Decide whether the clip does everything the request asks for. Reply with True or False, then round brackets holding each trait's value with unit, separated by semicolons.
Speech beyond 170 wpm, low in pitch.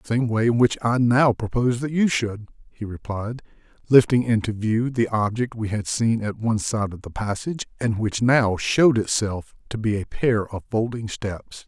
True (200 wpm; 115 Hz)